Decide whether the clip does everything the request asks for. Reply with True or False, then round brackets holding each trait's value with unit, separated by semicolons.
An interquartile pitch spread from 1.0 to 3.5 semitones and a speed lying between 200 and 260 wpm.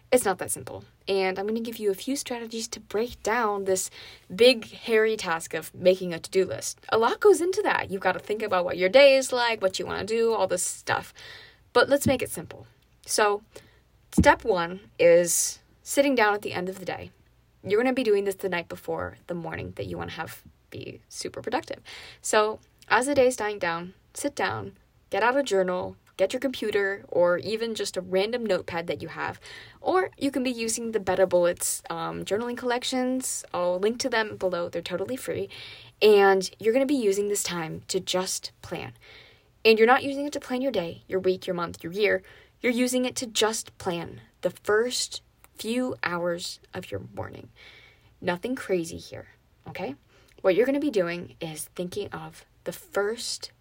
False (5.2 semitones; 205 wpm)